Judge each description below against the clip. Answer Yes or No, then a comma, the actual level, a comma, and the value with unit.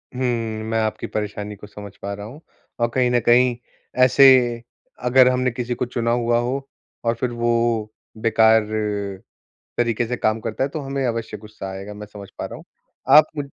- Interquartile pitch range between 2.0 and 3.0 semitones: Yes, average, 2.7 semitones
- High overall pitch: No, low, 115 Hz